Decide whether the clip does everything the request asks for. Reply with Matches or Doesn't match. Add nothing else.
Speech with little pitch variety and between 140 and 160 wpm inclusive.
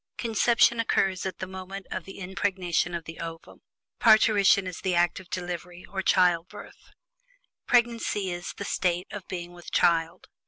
Matches